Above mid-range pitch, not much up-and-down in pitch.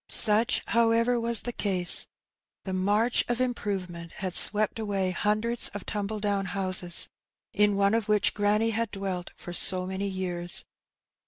No: high, 205 Hz; average, 3.0 semitones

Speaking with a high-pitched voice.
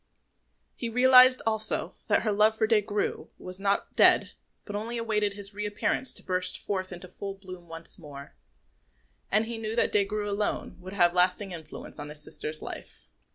Yes: high, 205 Hz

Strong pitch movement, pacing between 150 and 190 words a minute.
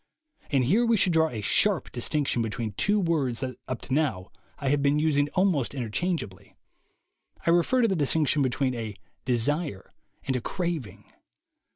Yes: wide, 5.7 semitones; average, 165 wpm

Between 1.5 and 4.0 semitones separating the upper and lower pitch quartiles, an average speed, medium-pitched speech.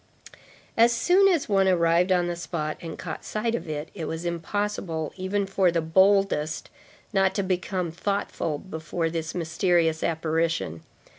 Yes: average, 3.2 semitones; average, 150 wpm; medium, 175 Hz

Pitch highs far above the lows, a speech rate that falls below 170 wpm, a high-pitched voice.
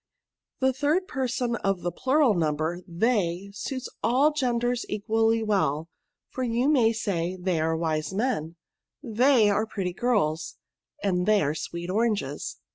Yes: wide, 6.1 semitones; average, 145 wpm; high, 210 Hz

